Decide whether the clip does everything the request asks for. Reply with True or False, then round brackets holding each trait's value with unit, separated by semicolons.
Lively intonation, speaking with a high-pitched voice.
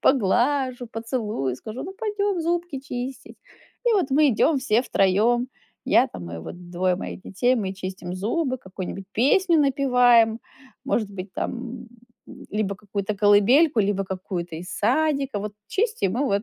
True (5.8 semitones; 230 Hz)